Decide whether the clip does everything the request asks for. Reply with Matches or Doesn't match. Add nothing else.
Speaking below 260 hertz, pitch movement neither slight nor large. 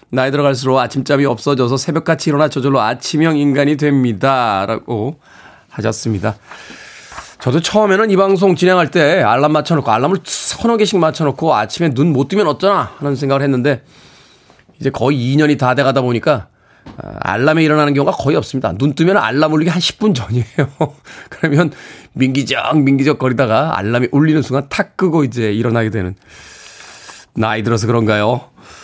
Matches